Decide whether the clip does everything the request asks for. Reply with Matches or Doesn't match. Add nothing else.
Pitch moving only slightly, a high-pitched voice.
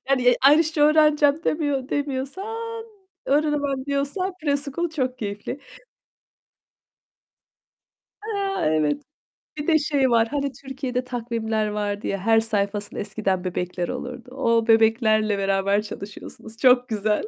Doesn't match